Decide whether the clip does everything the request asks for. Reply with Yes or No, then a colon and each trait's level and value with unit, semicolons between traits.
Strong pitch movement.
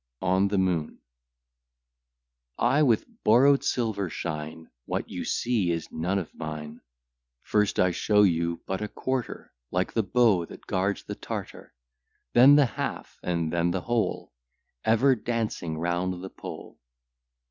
No: average, 5.0 semitones